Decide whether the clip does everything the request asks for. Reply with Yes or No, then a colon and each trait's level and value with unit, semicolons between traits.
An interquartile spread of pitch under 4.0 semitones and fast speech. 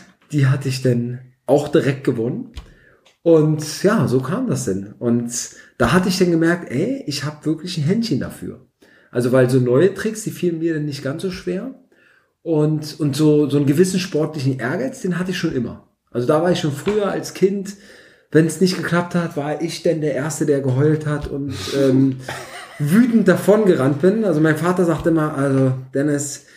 No: average, 4.4 semitones; fast, 195 wpm